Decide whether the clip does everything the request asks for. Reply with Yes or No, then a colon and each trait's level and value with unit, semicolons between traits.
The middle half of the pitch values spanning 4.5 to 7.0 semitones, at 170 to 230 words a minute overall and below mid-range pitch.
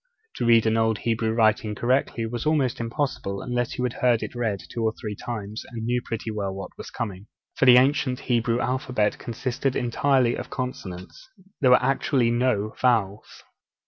No: narrow, 2.5 semitones; average, 175 wpm; low, 120 Hz